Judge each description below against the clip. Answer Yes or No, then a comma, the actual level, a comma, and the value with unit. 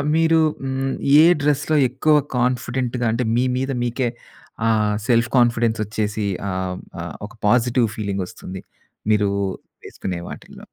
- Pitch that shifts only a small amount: No, average, 3.8 semitones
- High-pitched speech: No, low, 120 Hz